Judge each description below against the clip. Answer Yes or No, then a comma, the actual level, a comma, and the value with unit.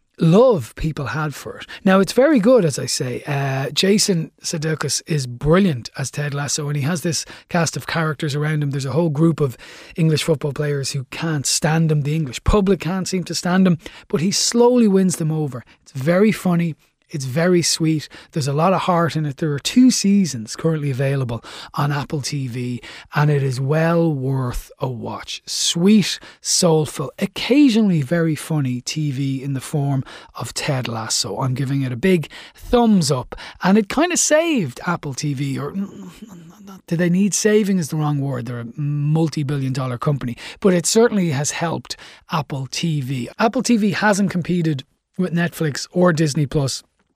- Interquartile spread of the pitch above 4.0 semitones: Yes, average, 4.4 semitones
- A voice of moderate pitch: Yes, medium, 160 Hz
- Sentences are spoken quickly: No, average, 175 wpm